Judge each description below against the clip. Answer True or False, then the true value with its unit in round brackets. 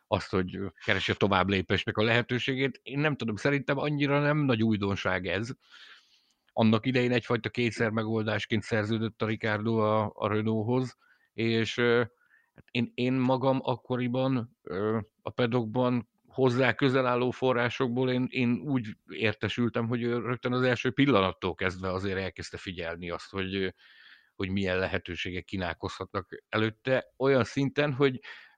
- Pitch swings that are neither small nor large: True (3.2 semitones)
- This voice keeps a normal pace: True (130 wpm)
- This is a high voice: False (115 Hz)